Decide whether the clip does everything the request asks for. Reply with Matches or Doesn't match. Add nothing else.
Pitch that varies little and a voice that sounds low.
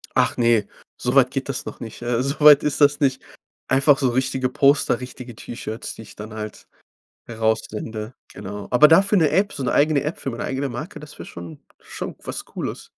Doesn't match